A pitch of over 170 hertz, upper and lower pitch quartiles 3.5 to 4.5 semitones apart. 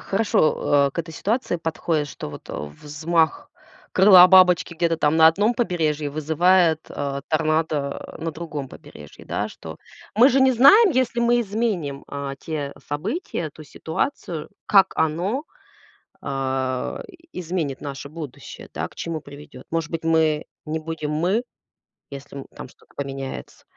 No: medium, 160 Hz; average, 4.1 semitones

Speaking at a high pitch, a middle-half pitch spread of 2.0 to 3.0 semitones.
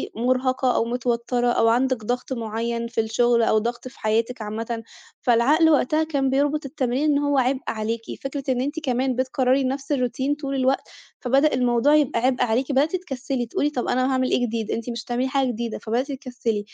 Yes: very high, 255 Hz; narrow, 2.5 semitones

